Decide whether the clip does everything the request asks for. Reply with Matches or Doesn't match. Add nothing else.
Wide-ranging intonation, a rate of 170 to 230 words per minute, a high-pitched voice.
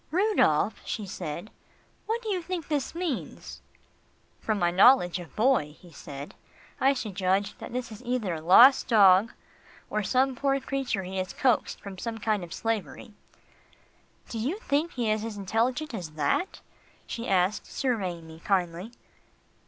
Doesn't match